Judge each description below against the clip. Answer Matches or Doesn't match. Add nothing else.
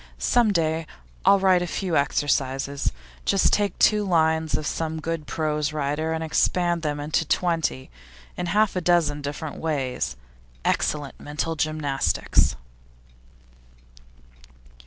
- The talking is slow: Matches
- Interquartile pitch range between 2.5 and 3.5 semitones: Matches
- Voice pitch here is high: Doesn't match